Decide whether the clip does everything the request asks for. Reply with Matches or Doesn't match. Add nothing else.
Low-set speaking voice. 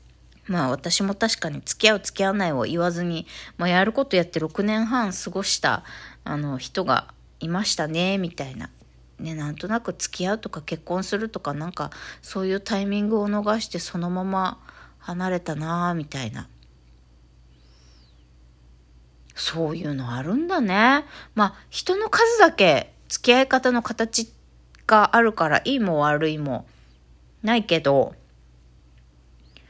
Doesn't match